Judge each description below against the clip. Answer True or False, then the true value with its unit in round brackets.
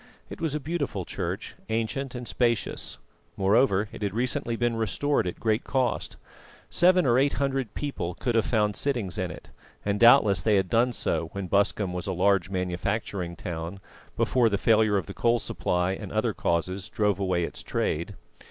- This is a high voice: False (105 Hz)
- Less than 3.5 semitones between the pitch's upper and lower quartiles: False (4.4 semitones)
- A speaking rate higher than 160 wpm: True (180 wpm)